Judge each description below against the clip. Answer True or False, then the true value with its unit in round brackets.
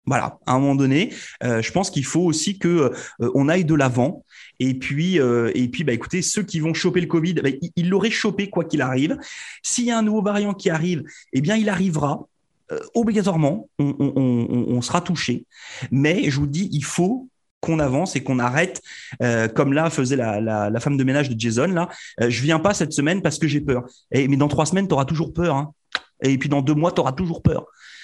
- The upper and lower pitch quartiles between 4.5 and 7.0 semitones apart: True (4.8 semitones)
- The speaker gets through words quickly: True (240 wpm)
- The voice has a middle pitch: True (150 Hz)